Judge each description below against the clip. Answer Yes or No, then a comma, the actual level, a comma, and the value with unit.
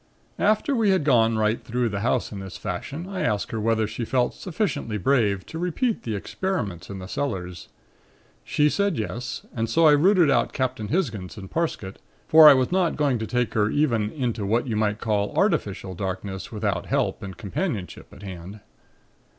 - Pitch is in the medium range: No, low, 115 Hz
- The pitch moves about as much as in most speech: No, wide, 6.8 semitones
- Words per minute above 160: Yes, average, 185 wpm